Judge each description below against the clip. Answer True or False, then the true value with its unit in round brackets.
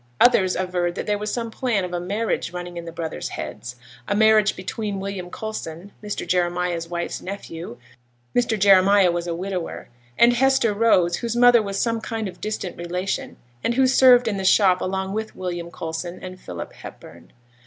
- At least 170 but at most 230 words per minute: True (180 wpm)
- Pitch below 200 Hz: True (190 Hz)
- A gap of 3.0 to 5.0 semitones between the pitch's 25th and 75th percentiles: True (3.8 semitones)